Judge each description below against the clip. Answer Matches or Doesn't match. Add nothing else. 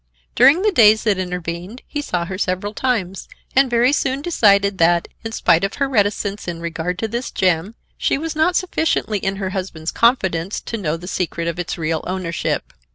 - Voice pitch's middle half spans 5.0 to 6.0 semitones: Matches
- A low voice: Doesn't match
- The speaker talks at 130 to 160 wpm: Doesn't match